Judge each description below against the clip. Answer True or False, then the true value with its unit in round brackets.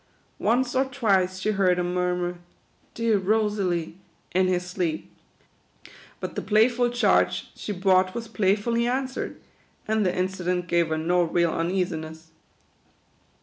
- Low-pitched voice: False (185 Hz)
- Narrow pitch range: False (3.6 semitones)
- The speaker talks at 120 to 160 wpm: True (145 wpm)